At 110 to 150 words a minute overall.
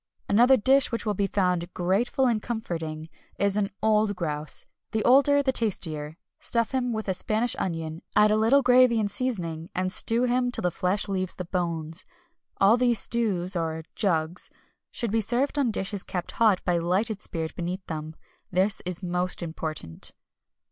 No: average, 170 wpm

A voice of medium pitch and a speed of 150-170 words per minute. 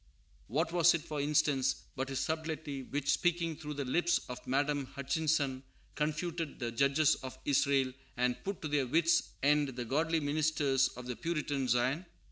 Yes: medium, 145 Hz; average, 165 wpm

